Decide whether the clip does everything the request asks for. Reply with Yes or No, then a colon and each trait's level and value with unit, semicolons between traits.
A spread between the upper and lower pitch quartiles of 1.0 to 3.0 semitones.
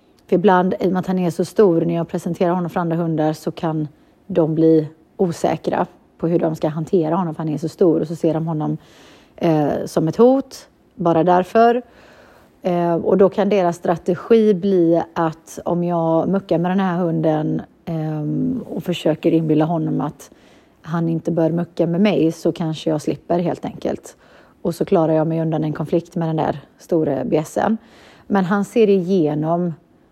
Yes: narrow, 2.5 semitones